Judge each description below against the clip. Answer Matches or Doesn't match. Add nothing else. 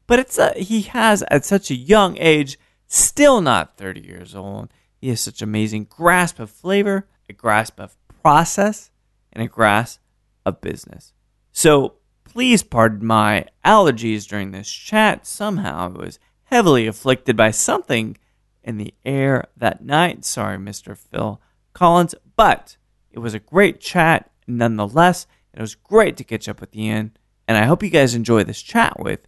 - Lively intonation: Matches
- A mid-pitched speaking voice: Doesn't match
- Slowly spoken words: Doesn't match